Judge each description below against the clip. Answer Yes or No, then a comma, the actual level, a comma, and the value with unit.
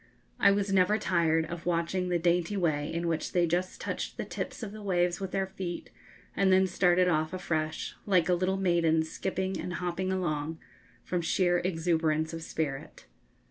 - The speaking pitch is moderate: Yes, medium, 175 Hz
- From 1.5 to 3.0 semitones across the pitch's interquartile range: Yes, narrow, 2.4 semitones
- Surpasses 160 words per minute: Yes, average, 180 wpm